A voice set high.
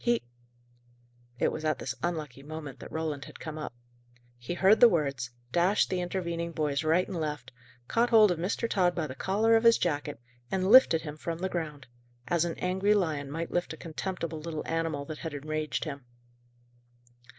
No: medium, 160 Hz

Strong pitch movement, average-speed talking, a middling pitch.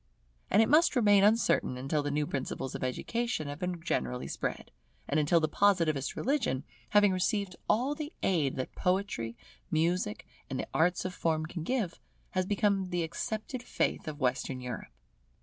Yes: wide, 6.0 semitones; average, 165 wpm; medium, 175 Hz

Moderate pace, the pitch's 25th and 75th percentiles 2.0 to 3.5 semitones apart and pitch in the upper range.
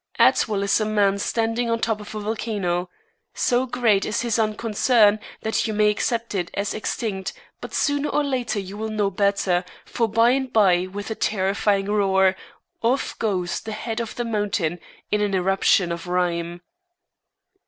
Yes: average, 170 wpm; average, 2.8 semitones; high, 210 Hz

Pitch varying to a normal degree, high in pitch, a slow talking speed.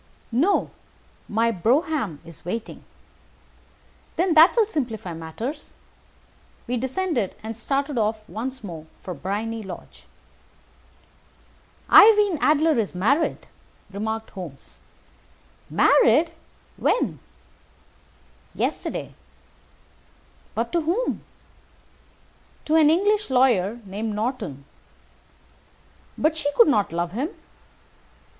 No: wide, 7.3 semitones; high, 235 Hz; slow, 95 wpm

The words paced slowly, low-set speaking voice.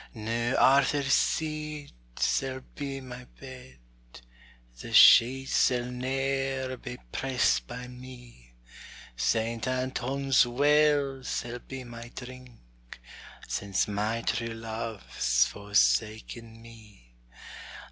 Yes: slow, 95 wpm; low, 125 Hz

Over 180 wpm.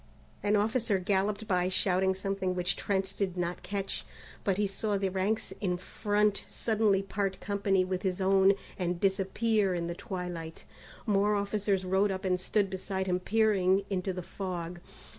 No: average, 160 wpm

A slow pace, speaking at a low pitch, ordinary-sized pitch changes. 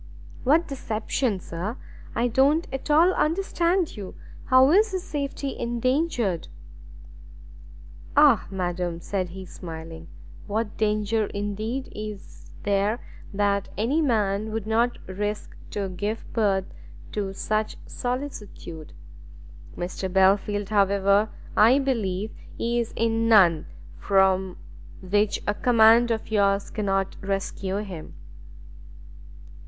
No: slow, 105 wpm; high, 210 Hz; average, 3.6 semitones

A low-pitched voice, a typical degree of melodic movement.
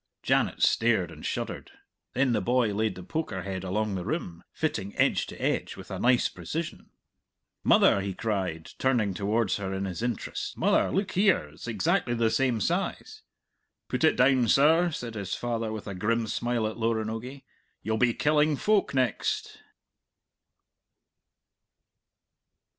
Yes: low, 115 Hz; average, 4.3 semitones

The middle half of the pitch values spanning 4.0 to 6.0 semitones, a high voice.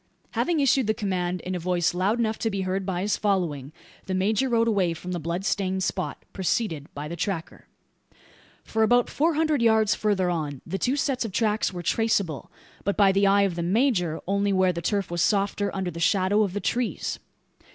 No: average, 3.5 semitones; high, 195 Hz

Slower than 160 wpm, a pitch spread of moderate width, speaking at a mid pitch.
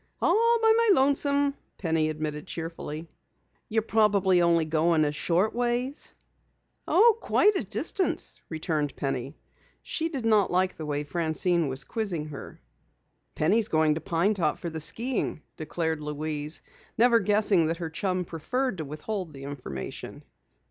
No: average, 150 wpm; wide, 6.4 semitones; medium, 170 Hz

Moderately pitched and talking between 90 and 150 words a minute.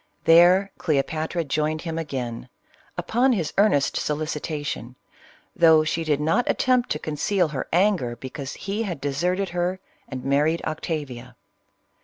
Yes: medium, 155 Hz; slow, 135 wpm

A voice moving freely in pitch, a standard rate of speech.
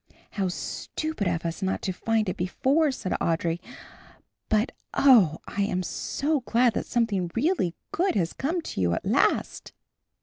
Yes: wide, 6.9 semitones; average, 160 wpm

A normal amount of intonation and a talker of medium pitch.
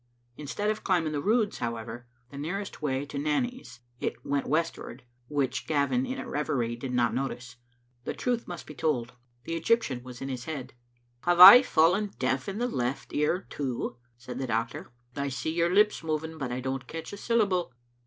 No: wide, 6.1 semitones; medium, 145 Hz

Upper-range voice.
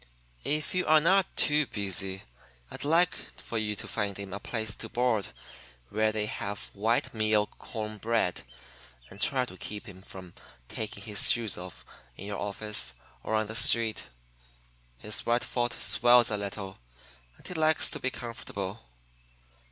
No: low, 110 Hz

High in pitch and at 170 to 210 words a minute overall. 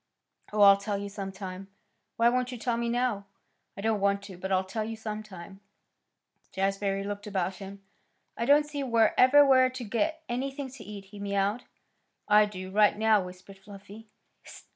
Yes: high, 210 Hz; average, 180 wpm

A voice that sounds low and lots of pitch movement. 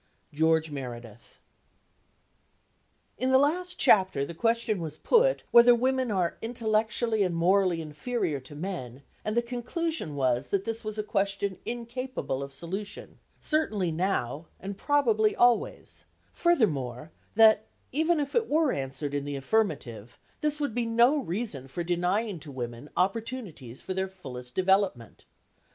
No: high, 195 Hz; wide, 8.2 semitones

